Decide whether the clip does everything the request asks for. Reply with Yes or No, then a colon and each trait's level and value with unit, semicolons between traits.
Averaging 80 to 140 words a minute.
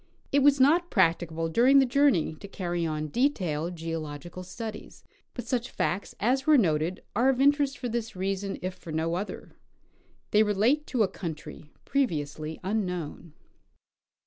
No: average, 150 wpm